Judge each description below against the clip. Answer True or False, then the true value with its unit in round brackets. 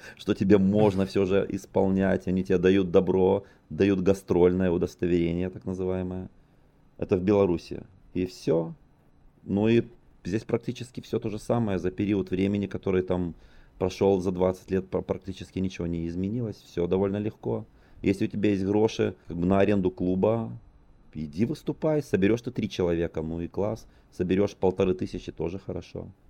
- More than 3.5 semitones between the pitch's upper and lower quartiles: False (2.4 semitones)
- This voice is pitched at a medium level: False (95 Hz)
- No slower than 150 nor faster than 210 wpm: True (155 wpm)